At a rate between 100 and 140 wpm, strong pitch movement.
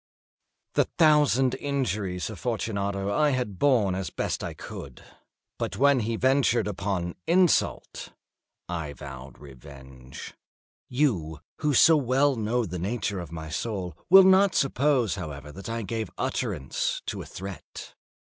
Yes: slow, 135 wpm; wide, 7.5 semitones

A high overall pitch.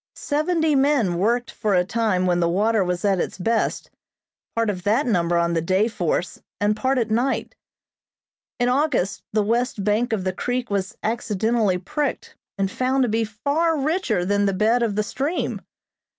Yes: high, 220 Hz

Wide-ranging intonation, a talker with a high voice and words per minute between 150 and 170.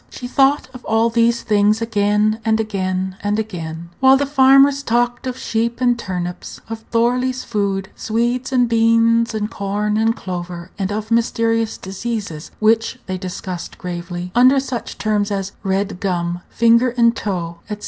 No: average, 3.5 semitones; high, 220 Hz; average, 160 wpm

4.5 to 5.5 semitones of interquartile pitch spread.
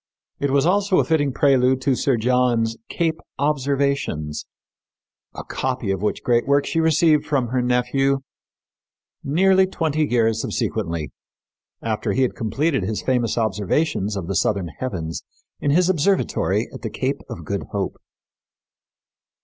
Yes: average, 5.0 semitones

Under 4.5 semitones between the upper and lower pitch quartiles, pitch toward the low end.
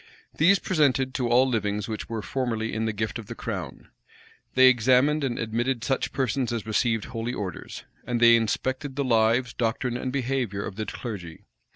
Yes: average, 2.8 semitones; low, 120 Hz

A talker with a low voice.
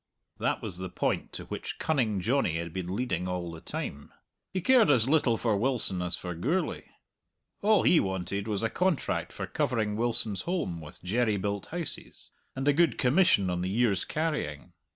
Yes: low, 110 Hz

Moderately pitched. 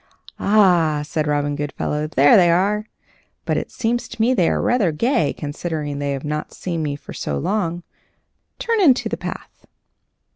Yes: medium, 165 Hz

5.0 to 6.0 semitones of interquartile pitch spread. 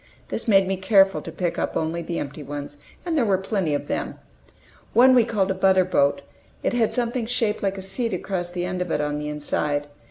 Yes: average, 5.3 semitones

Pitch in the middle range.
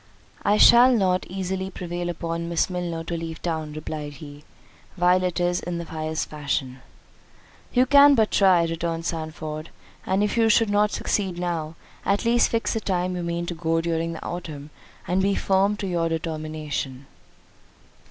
Yes: medium, 170 Hz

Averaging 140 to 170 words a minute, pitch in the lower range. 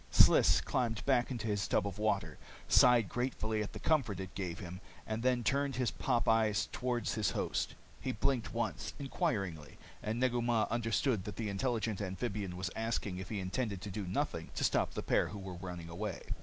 No: average, 195 wpm; low, 110 Hz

